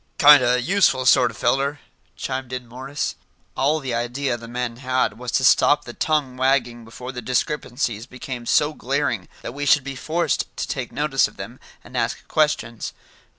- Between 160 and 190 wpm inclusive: Yes, average, 180 wpm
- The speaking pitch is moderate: No, low, 130 Hz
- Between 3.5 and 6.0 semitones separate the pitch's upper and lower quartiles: No, average, 2.7 semitones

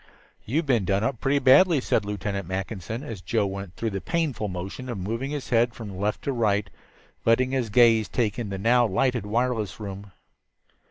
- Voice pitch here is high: No, low, 110 Hz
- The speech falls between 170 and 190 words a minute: Yes, average, 185 wpm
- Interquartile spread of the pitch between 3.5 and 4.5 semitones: Yes, average, 4.0 semitones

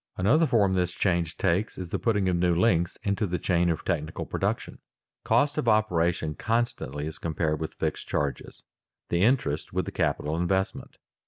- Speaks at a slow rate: No, average, 170 wpm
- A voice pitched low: Yes, very low, 90 Hz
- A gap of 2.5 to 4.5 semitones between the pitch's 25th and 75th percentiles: Yes, average, 4.2 semitones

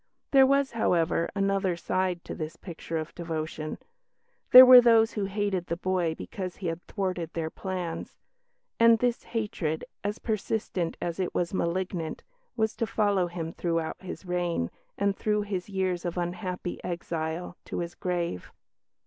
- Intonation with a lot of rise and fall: No, average, 3.3 semitones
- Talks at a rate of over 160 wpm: No, average, 155 wpm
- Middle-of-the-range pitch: Yes, medium, 180 Hz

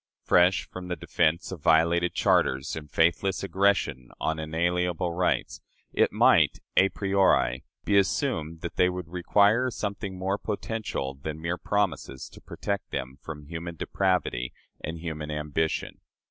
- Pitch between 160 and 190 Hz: No, very low, 85 Hz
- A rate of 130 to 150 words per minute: Yes, average, 140 wpm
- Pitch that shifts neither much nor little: Yes, average, 3.5 semitones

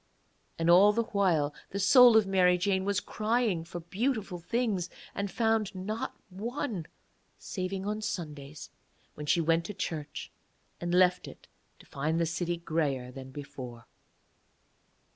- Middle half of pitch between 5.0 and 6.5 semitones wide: No, average, 4.2 semitones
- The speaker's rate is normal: Yes, average, 145 wpm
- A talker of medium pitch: Yes, medium, 180 Hz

